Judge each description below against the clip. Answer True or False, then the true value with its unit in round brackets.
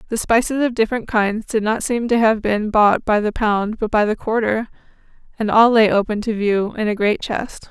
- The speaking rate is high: True (225 wpm)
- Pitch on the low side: False (220 Hz)